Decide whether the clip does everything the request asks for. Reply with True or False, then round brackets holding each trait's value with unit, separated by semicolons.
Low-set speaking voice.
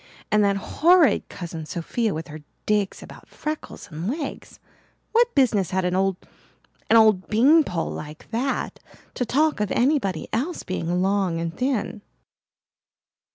False (210 Hz)